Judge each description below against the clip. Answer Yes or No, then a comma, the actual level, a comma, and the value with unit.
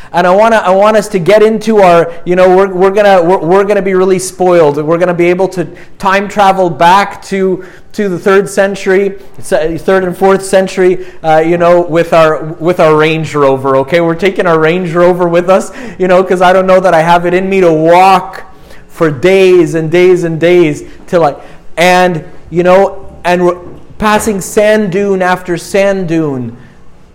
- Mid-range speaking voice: Yes, medium, 180 Hz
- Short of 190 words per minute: No, average, 200 wpm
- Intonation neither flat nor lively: No, narrow, 2.2 semitones